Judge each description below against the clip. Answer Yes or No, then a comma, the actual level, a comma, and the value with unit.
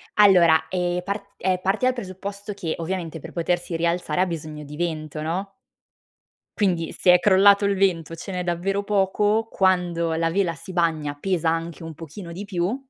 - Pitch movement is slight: No, average, 3.0 semitones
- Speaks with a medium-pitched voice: Yes, medium, 180 Hz